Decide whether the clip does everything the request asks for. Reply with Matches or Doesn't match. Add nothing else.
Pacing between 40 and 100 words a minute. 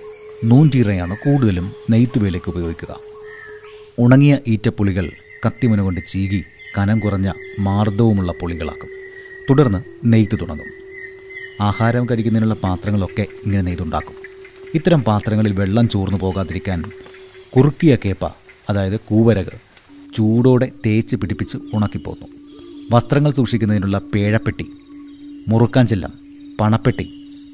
Matches